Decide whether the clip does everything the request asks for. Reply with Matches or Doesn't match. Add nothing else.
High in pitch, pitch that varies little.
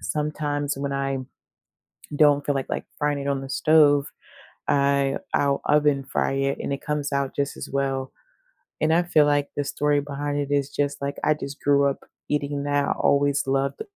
Doesn't match